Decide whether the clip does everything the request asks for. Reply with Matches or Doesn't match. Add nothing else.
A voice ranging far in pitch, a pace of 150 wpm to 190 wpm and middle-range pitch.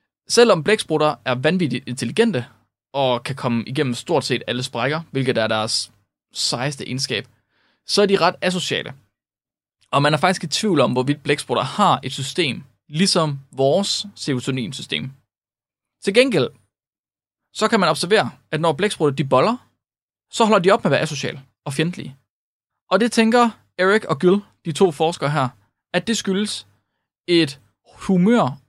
Matches